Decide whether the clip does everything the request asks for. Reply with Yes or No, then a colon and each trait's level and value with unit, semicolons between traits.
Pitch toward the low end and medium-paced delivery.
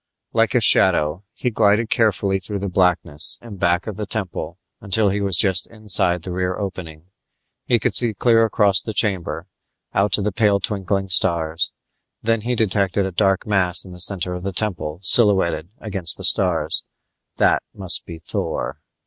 Yes: very low, 95 Hz; average, 175 wpm